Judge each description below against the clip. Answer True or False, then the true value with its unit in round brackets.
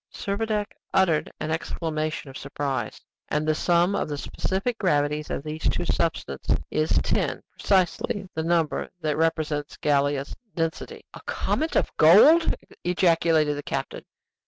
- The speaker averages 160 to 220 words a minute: False (135 wpm)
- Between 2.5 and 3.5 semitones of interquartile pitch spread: True (3.2 semitones)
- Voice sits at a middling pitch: True (160 Hz)